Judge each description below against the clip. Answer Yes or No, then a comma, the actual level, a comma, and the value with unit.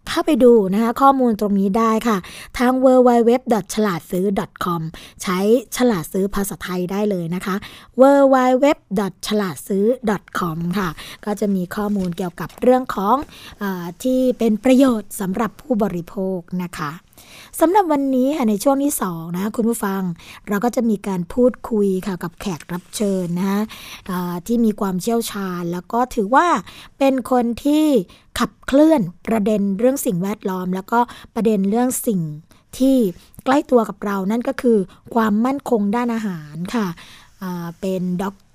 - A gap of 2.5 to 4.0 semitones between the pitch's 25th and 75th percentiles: No, average, 4.6 semitones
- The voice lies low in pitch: No, high, 210 Hz